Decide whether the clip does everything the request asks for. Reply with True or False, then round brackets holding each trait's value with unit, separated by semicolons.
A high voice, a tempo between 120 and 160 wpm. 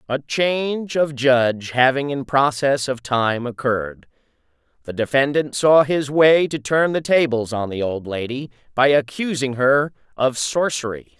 False (135 Hz; 150 wpm)